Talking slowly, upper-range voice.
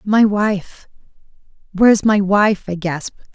Yes: slow, 125 wpm; high, 200 Hz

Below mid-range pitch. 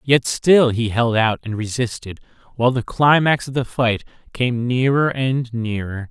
Yes: low, 120 Hz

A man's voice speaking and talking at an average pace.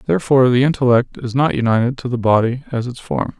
No: male; fast, 210 wpm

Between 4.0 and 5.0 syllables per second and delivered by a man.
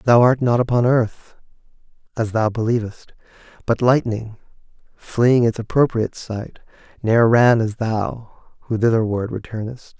Yes: 4.5 syllables/s; male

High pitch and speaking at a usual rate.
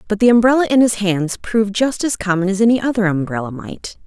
No: high, 205 Hz; fast, 220 wpm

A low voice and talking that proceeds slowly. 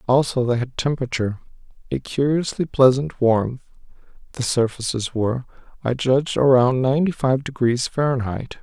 Yes: low, 130 Hz; slow, 120 wpm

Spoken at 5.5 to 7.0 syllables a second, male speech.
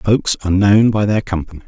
Yes: 6.2 syllables/s; male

